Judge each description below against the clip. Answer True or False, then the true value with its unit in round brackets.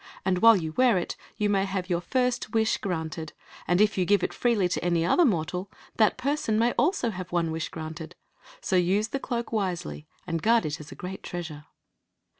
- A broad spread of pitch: False (4.7 semitones)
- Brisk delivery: True (210 wpm)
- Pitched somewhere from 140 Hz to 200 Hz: True (185 Hz)